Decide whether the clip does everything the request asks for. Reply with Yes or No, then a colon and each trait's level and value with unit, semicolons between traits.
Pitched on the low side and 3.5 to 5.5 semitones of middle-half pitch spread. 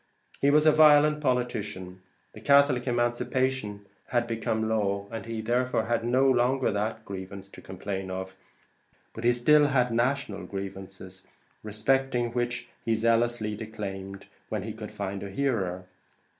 Yes: low, 115 Hz; average, 4.2 semitones